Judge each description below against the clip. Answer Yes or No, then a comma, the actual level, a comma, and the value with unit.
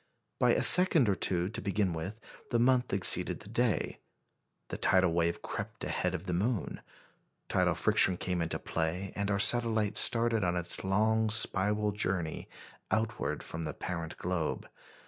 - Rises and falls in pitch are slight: No, average, 3.9 semitones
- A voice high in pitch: No, low, 100 Hz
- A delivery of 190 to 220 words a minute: No, average, 160 wpm